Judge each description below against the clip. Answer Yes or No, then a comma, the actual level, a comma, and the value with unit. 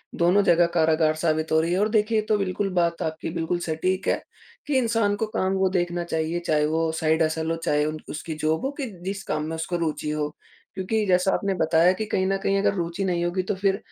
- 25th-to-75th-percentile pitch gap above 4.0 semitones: No, average, 3.5 semitones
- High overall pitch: No, medium, 175 Hz